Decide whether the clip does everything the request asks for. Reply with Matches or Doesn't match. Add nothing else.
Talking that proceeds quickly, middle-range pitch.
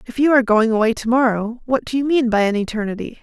Doesn't match